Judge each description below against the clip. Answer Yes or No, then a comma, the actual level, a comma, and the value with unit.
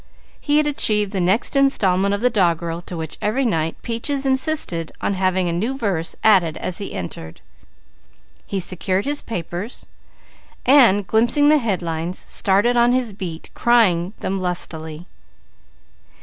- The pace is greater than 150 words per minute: No, average, 145 wpm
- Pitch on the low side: No, high, 195 Hz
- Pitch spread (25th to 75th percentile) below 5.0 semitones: No, wide, 5.5 semitones